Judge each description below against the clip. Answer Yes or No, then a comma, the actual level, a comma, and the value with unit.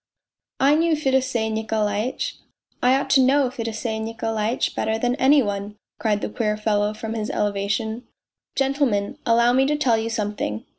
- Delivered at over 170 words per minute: Yes, average, 180 wpm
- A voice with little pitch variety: No, average, 3.6 semitones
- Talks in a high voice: Yes, high, 225 Hz